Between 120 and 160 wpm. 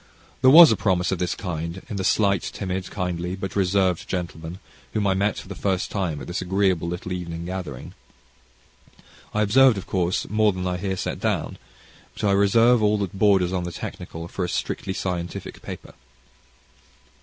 No: average, 180 wpm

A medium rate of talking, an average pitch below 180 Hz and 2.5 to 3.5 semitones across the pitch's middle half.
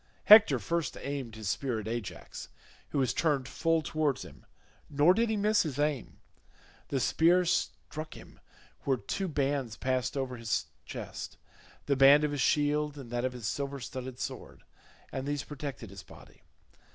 Yes: average, 160 wpm; medium, 140 Hz; average, 3.2 semitones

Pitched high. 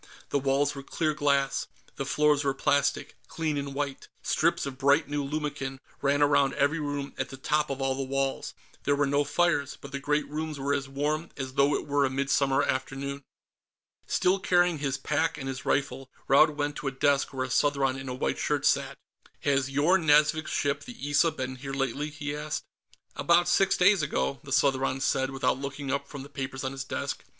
No: medium, 140 Hz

